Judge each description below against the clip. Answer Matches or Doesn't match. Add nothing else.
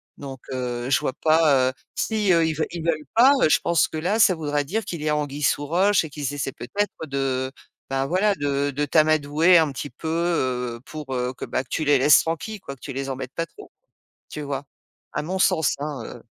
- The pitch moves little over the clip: Doesn't match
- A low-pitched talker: Doesn't match